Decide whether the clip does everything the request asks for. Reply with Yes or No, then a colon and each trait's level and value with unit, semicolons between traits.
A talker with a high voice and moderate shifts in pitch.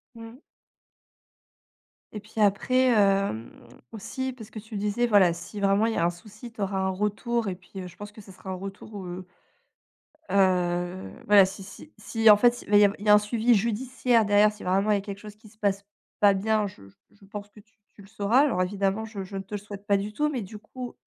No: high, 205 Hz; narrow, 2.1 semitones